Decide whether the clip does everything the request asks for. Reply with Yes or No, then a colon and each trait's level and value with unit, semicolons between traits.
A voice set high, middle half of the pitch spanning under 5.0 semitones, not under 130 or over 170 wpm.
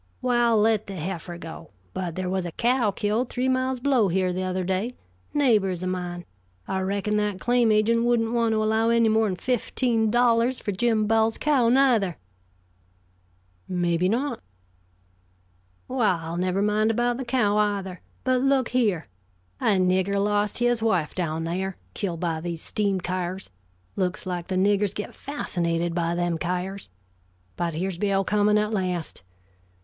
Yes: high, 205 Hz; average, 4.1 semitones; average, 160 wpm